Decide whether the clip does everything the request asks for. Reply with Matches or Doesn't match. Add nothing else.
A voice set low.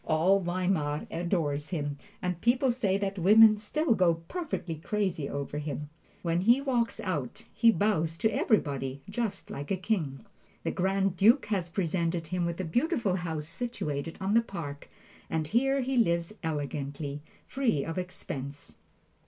Doesn't match